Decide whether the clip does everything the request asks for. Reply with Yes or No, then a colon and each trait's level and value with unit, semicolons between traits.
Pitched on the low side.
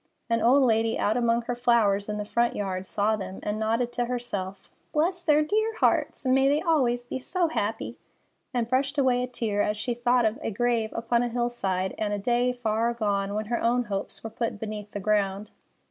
No: high, 235 Hz